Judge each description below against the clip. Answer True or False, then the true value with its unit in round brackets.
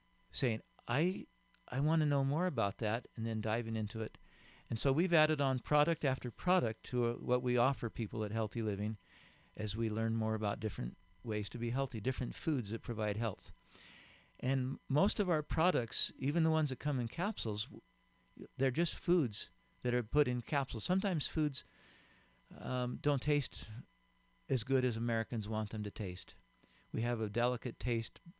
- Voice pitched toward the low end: True (120 Hz)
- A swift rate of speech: False (175 wpm)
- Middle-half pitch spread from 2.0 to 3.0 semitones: False (4.6 semitones)